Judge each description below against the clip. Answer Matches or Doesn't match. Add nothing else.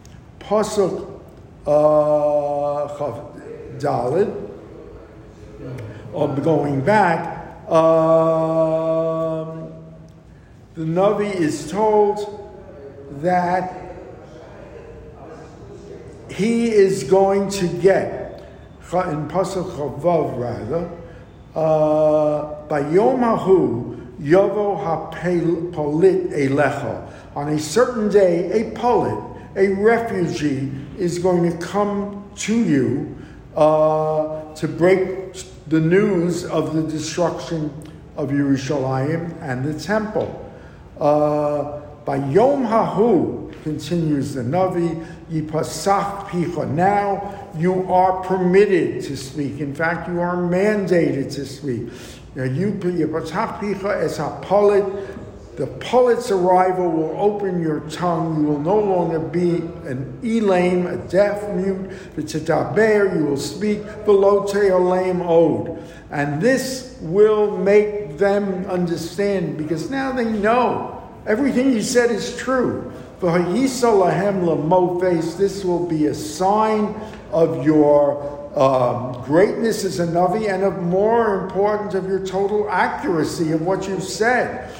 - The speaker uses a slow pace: Matches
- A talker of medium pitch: Matches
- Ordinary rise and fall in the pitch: Matches